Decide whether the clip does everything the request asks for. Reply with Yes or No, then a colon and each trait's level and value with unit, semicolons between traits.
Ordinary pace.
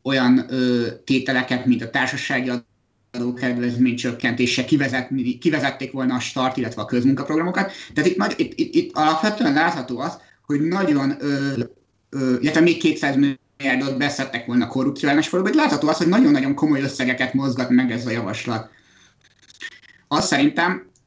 Yes: average, 140 wpm